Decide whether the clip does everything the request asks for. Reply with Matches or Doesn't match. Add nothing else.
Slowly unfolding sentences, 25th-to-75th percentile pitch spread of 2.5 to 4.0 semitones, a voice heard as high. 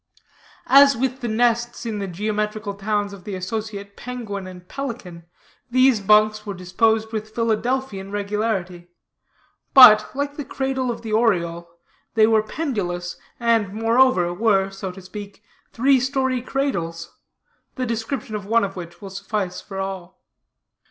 Doesn't match